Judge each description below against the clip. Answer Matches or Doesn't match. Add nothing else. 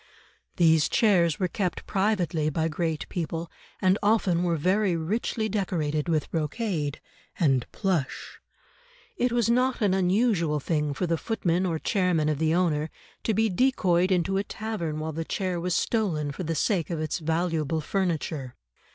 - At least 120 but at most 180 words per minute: Matches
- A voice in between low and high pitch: Matches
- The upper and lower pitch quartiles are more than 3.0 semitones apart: Matches